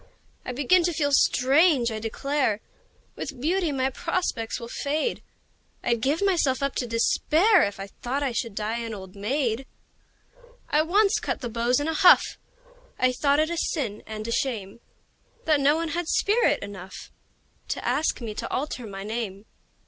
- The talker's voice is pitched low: No, very high, 265 Hz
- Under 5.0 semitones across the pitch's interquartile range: No, wide, 5.6 semitones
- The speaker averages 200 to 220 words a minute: No, average, 170 wpm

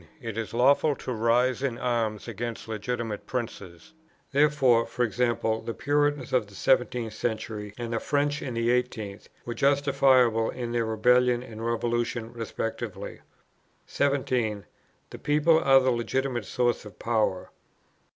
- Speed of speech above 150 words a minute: No, slow, 135 wpm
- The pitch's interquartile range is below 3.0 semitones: Yes, narrow, 2.5 semitones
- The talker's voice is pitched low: Yes, low, 120 Hz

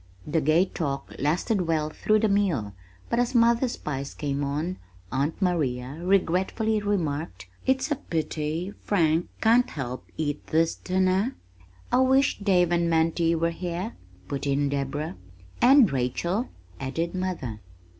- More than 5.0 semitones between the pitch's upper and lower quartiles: Yes, wide, 5.6 semitones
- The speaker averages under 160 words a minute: Yes, slow, 135 wpm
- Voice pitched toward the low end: No, medium, 170 Hz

